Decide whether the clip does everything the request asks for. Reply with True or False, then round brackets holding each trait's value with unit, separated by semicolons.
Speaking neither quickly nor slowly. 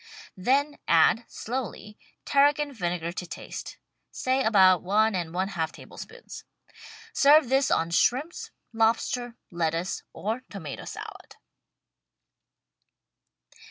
False (105 wpm)